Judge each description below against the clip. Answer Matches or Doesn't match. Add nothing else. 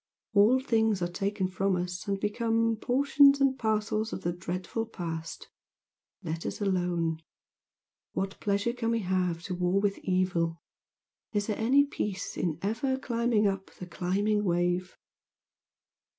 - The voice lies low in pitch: Doesn't match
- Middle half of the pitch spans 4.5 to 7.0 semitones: Doesn't match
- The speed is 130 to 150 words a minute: Matches